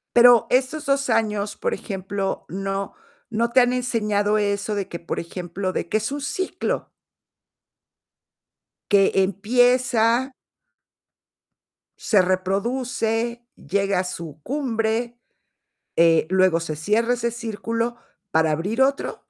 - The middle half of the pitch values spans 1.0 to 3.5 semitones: No, average, 3.9 semitones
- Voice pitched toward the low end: No, high, 215 Hz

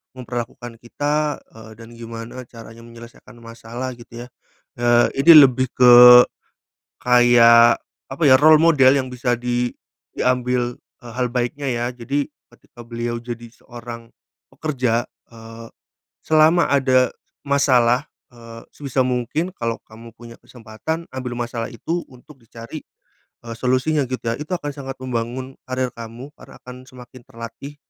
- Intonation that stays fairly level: Yes, narrow, 1.9 semitones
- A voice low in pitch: Yes, low, 125 Hz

